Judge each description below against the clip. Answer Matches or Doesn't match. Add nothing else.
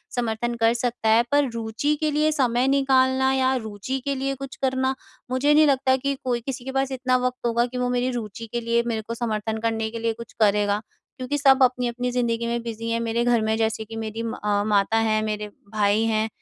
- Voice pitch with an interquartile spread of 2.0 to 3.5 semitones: Matches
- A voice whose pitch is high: Matches